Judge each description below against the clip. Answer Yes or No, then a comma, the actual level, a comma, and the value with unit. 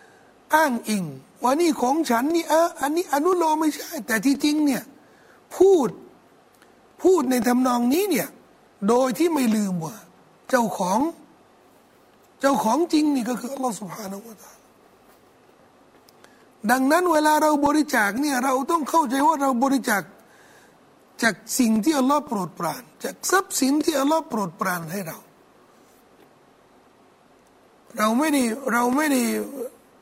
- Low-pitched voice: No, very high, 270 Hz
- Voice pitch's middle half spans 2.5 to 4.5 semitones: No, average, 5.3 semitones